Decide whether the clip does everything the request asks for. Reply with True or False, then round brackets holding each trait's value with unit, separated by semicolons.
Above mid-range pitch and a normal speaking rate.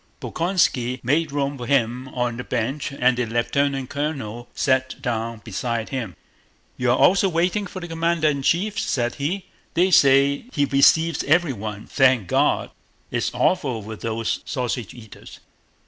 False (135 Hz; 145 wpm)